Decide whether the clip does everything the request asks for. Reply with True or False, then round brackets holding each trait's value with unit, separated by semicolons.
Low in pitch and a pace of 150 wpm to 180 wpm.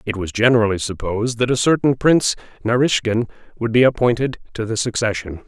True (115 Hz; 165 wpm)